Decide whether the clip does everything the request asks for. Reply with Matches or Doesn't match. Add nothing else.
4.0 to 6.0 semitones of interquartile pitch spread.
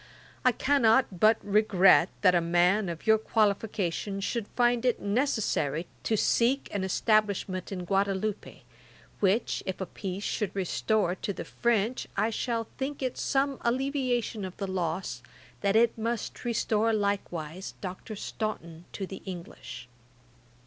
Doesn't match